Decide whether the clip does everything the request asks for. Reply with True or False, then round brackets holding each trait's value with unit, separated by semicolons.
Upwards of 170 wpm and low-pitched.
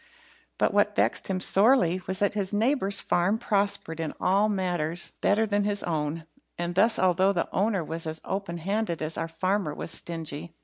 False (185 wpm; 185 Hz)